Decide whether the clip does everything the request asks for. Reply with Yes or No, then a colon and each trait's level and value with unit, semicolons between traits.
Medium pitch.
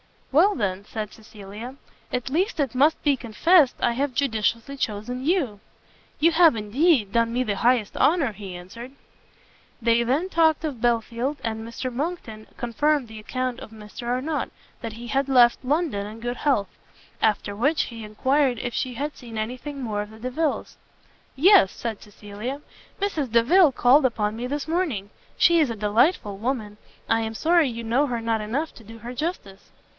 No: high, 240 Hz